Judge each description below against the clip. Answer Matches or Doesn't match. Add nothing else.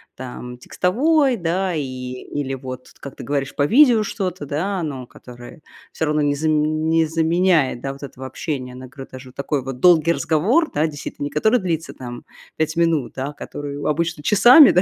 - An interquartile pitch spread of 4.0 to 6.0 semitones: Matches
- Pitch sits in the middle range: Matches